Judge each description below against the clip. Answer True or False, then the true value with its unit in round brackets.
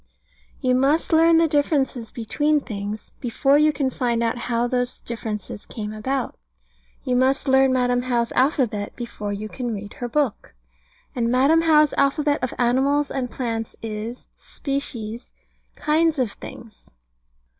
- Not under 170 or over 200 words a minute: False (145 wpm)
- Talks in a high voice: True (250 Hz)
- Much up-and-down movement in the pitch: False (3.5 semitones)